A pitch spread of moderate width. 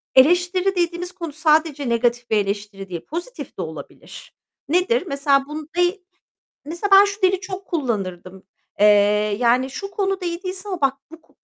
No: wide, 6.6 semitones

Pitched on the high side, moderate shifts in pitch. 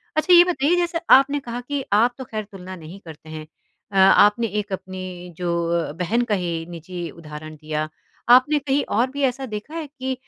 No: high, 210 Hz; wide, 7.8 semitones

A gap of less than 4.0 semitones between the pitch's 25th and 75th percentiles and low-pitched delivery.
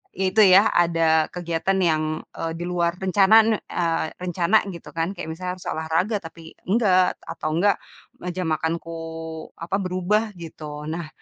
No: narrow, 2.5 semitones; medium, 175 Hz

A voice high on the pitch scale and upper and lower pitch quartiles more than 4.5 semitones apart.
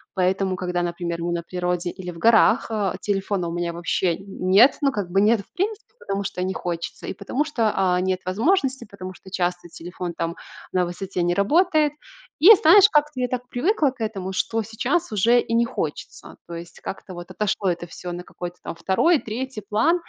Yes: high, 195 Hz; average, 5.2 semitones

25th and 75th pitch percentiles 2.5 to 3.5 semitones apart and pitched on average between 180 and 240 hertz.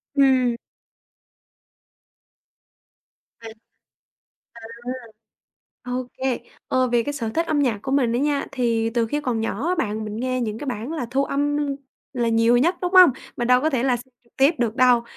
No: average, 3.1 semitones; very high, 250 Hz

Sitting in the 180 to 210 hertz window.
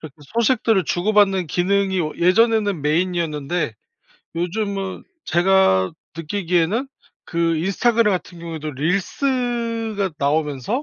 Yes: medium, 185 Hz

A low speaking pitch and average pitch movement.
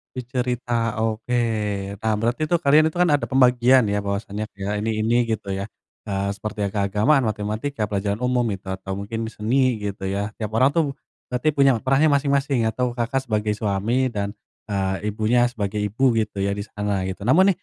Yes: low, 110 Hz; average, 3.8 semitones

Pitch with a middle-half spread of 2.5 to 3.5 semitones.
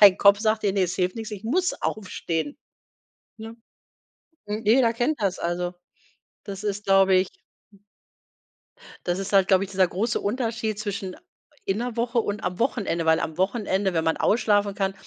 Yes: average, 2.9 semitones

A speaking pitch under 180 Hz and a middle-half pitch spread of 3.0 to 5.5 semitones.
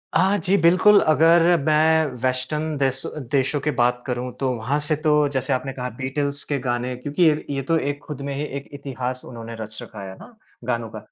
Yes: low, 135 Hz; average, 3.3 semitones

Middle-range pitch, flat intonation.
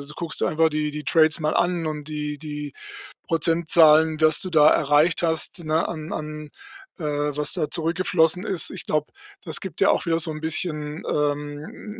Yes: medium, 155 Hz; narrow, 1.6 semitones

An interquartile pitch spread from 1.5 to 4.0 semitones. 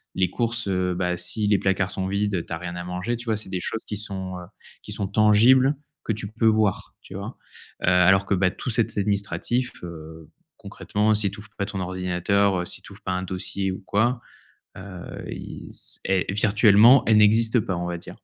Yes: average, 2.8 semitones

